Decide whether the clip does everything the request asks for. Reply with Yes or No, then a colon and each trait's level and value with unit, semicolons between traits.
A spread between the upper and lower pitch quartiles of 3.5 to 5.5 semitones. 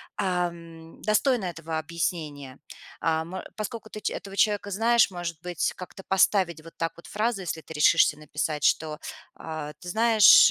Yes: average, 4.3 semitones